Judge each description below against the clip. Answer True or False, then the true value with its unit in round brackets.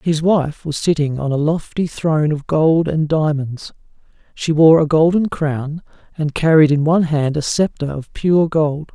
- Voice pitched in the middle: True (155 Hz)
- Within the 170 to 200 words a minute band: True (180 wpm)